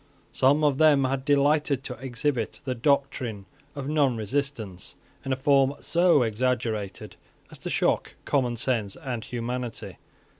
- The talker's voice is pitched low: Yes, low, 130 Hz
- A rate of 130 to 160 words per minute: Yes, slow, 135 wpm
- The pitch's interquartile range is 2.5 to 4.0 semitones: Yes, average, 3.2 semitones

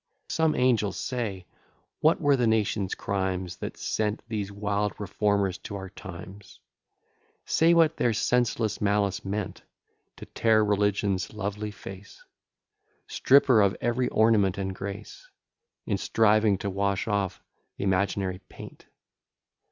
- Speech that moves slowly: Yes, slow, 125 wpm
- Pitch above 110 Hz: No, low, 105 Hz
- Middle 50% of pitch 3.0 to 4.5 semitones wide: No, narrow, 2.4 semitones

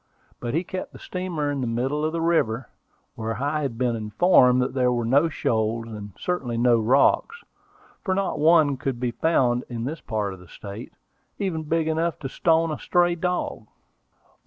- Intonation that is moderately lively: No, wide, 5.9 semitones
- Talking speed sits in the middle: Yes, average, 180 wpm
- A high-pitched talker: No, low, 135 Hz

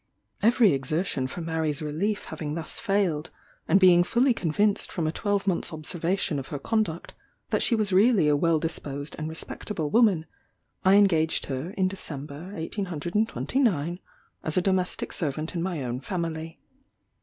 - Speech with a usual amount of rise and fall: Yes, average, 4.3 semitones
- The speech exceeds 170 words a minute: No, average, 150 wpm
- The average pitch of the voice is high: No, medium, 170 Hz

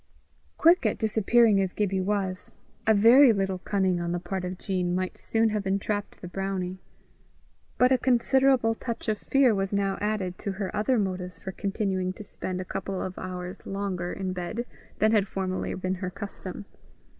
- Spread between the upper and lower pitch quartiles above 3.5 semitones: No, average, 2.7 semitones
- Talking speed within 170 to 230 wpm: Yes, average, 180 wpm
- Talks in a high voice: Yes, high, 195 Hz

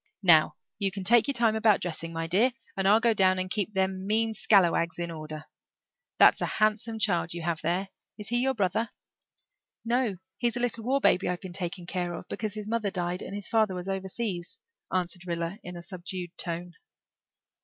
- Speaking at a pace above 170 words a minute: Yes, average, 195 wpm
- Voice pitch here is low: No, high, 190 Hz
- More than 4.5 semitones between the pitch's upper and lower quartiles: No, average, 3.9 semitones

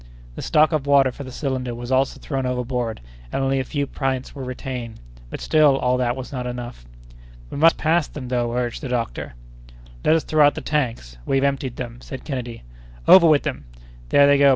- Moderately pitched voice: No, low, 130 Hz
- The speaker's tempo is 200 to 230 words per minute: Yes, fast, 205 wpm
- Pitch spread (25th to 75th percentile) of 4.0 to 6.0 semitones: No, narrow, 2.5 semitones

